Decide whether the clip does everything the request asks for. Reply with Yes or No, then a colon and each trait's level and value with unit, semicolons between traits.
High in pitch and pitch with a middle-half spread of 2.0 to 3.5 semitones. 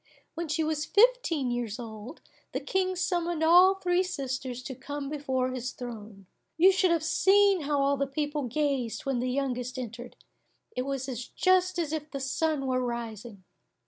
No: very high, 280 Hz; average, 5.2 semitones